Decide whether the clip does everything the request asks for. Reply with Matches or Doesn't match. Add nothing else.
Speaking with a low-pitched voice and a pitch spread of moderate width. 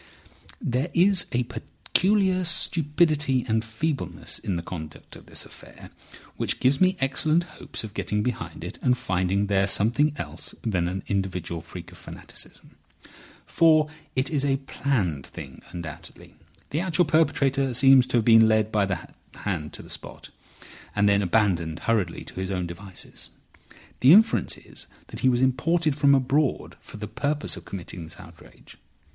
Doesn't match